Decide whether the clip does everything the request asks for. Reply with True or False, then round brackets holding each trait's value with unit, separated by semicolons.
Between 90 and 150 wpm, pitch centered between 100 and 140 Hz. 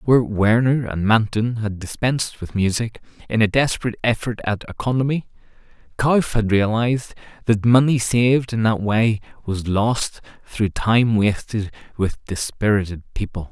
True (140 wpm; 110 Hz)